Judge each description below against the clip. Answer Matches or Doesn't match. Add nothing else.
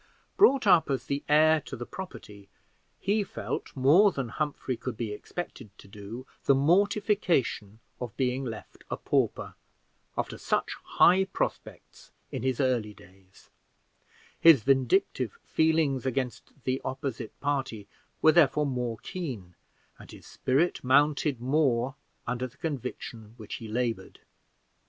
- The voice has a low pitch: Matches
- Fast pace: Doesn't match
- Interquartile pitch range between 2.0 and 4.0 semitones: Doesn't match